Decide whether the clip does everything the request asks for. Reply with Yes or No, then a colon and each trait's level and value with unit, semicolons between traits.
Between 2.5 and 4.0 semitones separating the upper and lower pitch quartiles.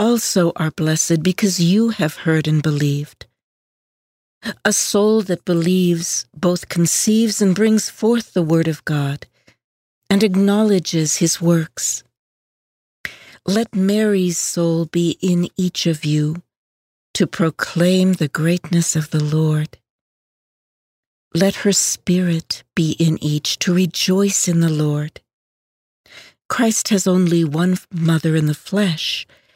Yes: average, 3.6 semitones